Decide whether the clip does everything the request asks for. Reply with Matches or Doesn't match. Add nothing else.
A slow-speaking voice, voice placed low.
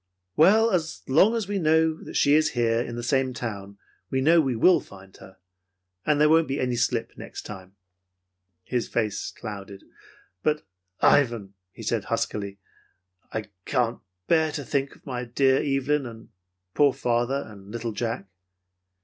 Doesn't match